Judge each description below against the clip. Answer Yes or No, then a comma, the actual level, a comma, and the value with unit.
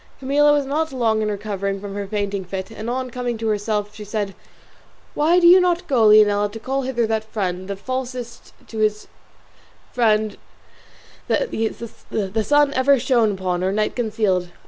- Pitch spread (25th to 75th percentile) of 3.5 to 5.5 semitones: Yes, average, 4.0 semitones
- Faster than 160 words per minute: Yes, average, 170 wpm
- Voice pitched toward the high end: Yes, high, 220 Hz